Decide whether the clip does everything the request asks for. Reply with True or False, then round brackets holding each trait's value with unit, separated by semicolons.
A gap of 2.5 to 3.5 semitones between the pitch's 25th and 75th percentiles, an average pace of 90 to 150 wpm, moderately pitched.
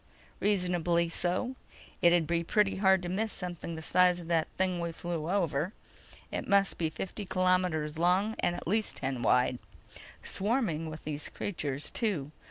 False (3.0 semitones; 160 wpm; 175 Hz)